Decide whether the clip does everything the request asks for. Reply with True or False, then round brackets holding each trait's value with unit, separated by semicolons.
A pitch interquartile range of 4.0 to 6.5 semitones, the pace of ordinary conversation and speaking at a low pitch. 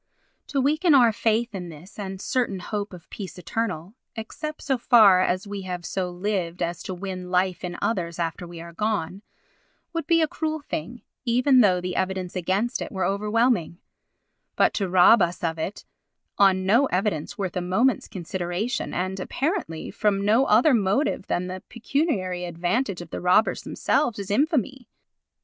False (4.6 semitones; 170 wpm; 195 Hz)